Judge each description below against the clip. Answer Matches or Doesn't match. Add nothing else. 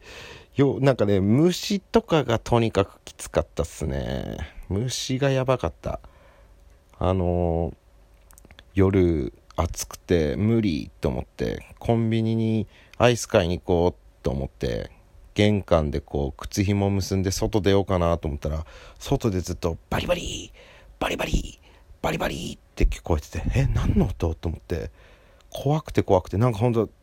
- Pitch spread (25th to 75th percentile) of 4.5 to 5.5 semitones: Matches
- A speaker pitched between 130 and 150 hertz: Doesn't match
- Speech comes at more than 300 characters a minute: Doesn't match